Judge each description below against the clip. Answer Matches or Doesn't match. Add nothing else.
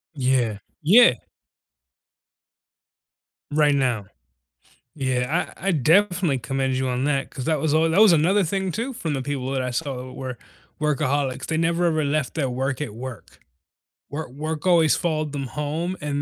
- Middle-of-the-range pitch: Matches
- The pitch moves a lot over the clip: Doesn't match